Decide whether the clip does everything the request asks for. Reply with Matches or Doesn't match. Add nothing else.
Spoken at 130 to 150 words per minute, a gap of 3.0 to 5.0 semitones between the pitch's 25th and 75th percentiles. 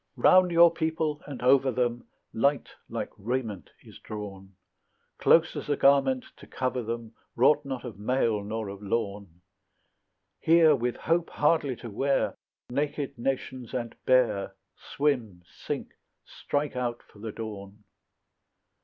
Matches